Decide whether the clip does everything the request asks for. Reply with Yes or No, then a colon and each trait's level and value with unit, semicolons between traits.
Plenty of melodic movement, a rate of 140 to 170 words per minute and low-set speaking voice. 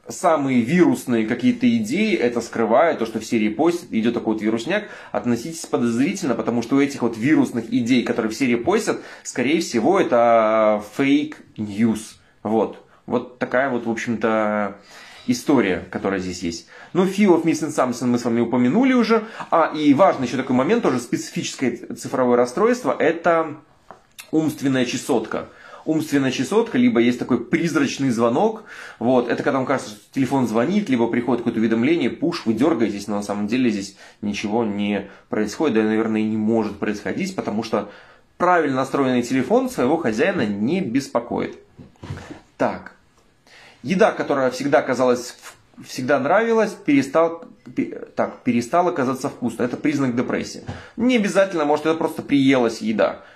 Yes: wide, 7.0 semitones; average, 150 wpm; low, 130 Hz